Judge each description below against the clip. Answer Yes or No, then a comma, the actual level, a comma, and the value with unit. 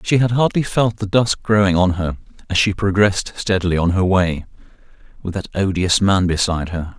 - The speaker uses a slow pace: No, average, 190 wpm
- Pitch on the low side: Yes, very low, 95 Hz